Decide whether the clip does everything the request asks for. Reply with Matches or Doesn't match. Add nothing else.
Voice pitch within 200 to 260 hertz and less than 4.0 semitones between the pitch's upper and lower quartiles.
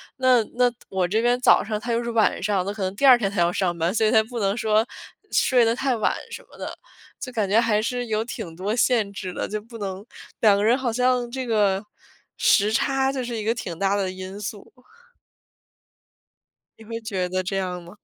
Matches